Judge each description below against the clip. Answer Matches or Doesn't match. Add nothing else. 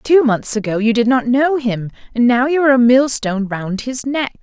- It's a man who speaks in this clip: Doesn't match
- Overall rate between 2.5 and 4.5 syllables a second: Doesn't match